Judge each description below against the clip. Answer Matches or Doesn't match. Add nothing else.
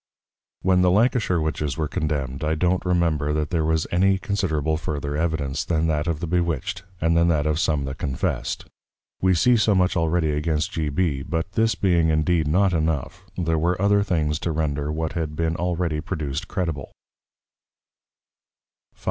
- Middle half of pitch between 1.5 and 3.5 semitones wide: Matches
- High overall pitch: Doesn't match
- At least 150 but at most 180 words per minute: Matches